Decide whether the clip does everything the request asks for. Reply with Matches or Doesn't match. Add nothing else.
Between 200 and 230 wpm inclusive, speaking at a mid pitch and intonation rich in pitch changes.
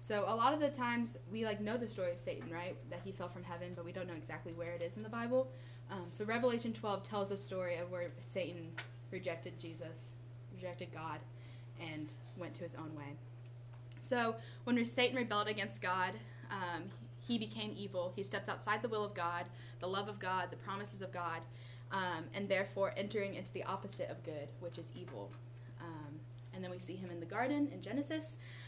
Matches